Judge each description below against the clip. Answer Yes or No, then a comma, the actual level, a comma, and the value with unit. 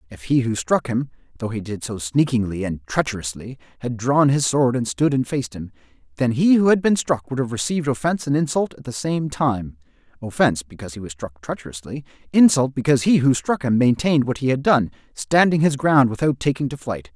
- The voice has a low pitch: Yes, low, 125 Hz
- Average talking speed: No, fast, 215 wpm